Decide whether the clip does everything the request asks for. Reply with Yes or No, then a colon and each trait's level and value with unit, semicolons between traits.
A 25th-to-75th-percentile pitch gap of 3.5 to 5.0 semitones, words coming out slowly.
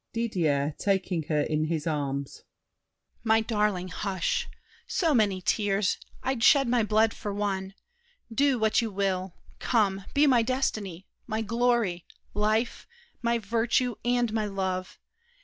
Yes: average, 3.9 semitones; slow, 130 wpm